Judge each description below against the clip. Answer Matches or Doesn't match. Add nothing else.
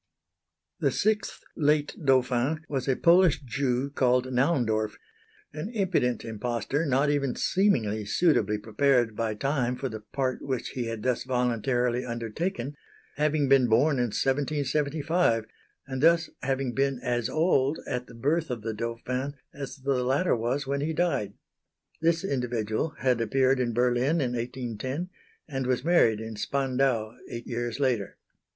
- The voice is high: Doesn't match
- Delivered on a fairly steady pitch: Doesn't match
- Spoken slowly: Doesn't match